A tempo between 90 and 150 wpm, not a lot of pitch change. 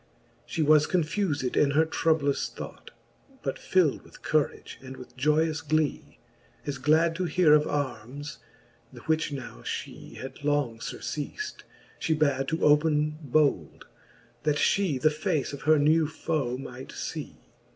Yes: average, 145 wpm; narrow, 2.1 semitones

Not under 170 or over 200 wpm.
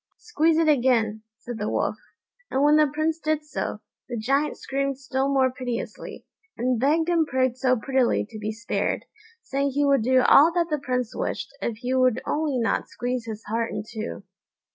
Yes: average, 185 wpm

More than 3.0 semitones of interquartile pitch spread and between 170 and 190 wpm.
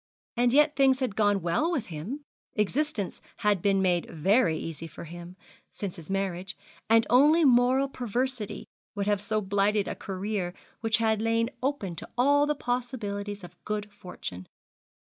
No: average, 4.7 semitones; average, 160 wpm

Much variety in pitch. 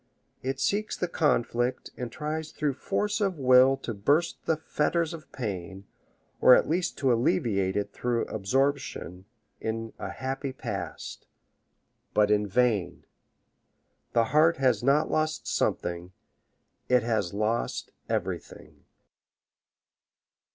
Yes: wide, 5.9 semitones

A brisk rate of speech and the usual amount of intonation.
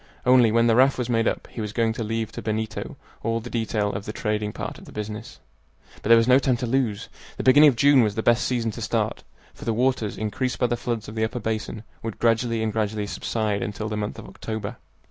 No: fast, 245 wpm; narrow, 2.0 semitones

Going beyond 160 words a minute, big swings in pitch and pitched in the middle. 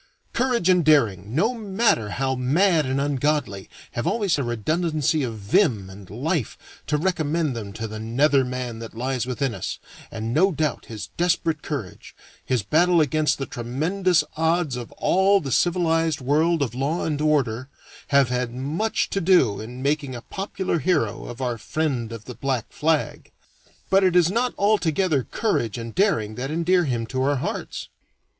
Yes: average, 170 wpm; wide, 6.0 semitones; medium, 145 Hz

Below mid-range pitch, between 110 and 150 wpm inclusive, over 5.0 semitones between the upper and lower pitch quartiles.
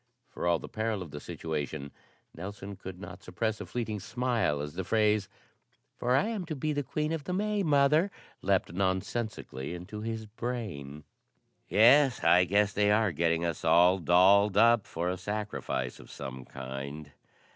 No: low, 100 Hz; average, 160 wpm; wide, 5.4 semitones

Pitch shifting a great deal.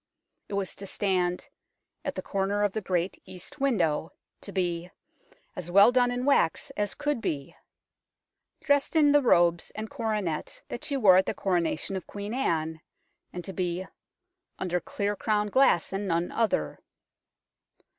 No: average, 5.0 semitones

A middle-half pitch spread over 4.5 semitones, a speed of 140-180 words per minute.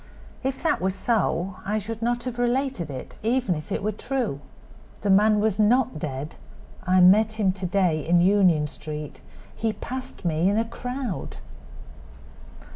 Yes: average, 5.1 semitones; average, 160 wpm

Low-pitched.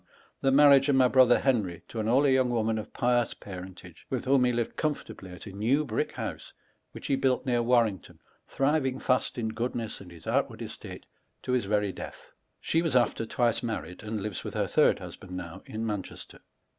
Yes: low, 120 Hz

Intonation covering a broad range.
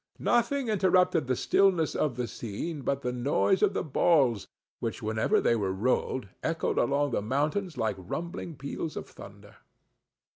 Yes: wide, 6.4 semitones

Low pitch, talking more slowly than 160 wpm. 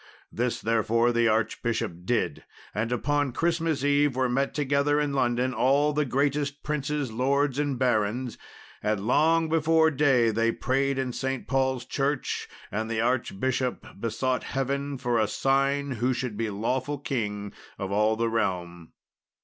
Yes: low, 130 Hz; average, 150 wpm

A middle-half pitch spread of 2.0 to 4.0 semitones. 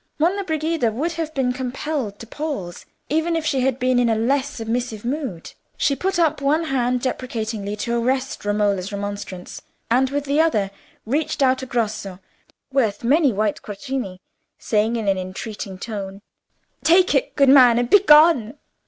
No: average, 5.3 semitones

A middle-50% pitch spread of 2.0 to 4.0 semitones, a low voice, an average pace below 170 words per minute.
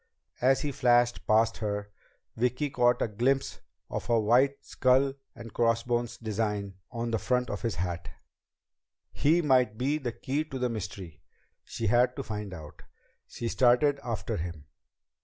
Yes: average, 3.4 semitones; low, 120 Hz; average, 155 wpm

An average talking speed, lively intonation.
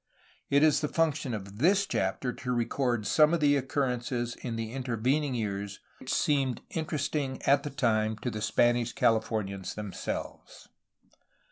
No: average, 150 wpm; average, 4.5 semitones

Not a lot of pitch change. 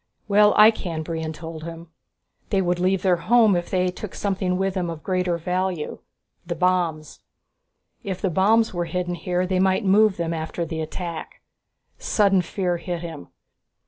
Yes: narrow, 2.3 semitones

